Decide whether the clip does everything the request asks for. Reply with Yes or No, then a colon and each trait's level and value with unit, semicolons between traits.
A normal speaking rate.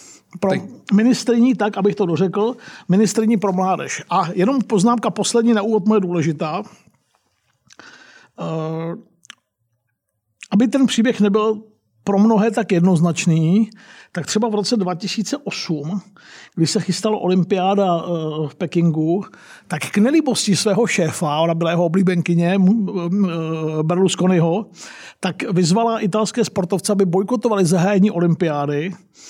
No: slow, 110 wpm